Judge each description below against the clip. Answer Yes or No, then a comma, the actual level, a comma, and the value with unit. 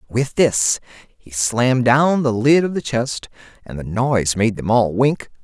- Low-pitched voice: Yes, low, 120 Hz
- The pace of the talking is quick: No, average, 190 wpm